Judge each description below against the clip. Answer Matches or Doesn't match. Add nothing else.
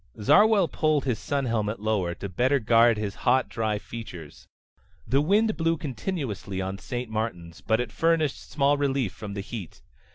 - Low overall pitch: Matches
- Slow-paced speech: Doesn't match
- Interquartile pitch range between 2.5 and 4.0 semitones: Doesn't match